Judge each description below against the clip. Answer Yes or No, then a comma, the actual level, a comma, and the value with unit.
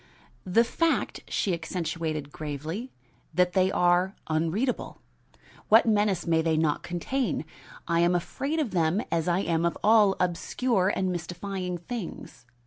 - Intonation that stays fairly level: No, average, 3.8 semitones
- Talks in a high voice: No, medium, 180 Hz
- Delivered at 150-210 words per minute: No, slow, 135 wpm